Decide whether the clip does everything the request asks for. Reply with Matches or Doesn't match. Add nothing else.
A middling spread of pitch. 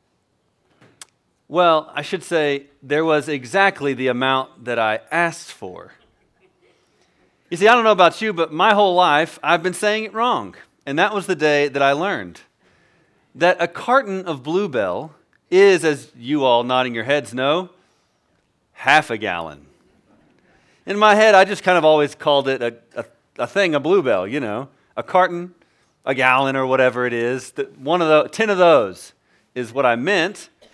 Doesn't match